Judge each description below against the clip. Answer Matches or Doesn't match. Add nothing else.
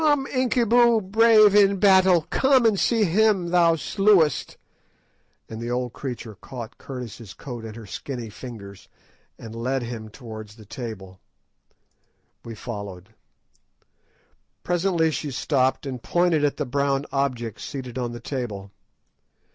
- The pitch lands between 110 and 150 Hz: Matches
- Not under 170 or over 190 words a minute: Doesn't match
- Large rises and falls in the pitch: Matches